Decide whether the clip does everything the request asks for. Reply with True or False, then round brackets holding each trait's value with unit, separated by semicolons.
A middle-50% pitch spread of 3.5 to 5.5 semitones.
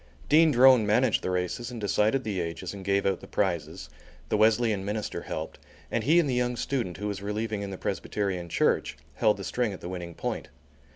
True (4.0 semitones)